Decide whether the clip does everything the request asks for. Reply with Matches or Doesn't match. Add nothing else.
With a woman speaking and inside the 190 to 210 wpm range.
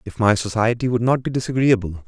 Doesn't match